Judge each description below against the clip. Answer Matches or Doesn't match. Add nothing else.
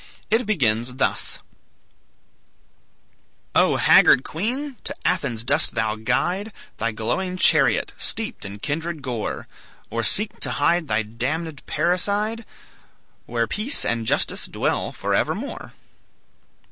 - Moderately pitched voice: Matches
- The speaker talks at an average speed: Doesn't match